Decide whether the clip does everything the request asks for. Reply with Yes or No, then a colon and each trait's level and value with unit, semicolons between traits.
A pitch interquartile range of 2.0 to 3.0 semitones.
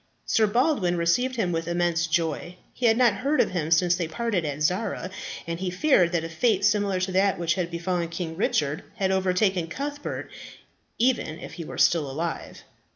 No: average, 3.7 semitones